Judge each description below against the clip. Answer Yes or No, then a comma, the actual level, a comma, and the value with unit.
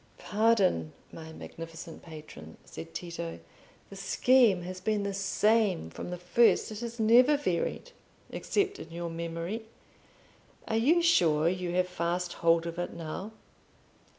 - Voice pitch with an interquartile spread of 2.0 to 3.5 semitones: No, average, 4.9 semitones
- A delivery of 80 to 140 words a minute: Yes, slow, 135 wpm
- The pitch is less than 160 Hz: No, medium, 180 Hz